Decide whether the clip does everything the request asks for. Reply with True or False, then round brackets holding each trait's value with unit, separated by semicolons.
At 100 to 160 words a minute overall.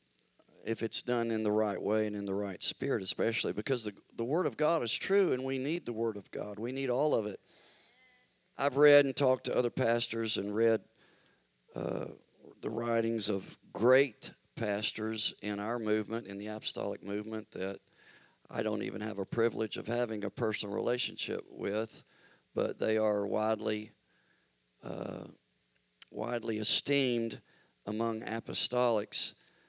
True (155 wpm)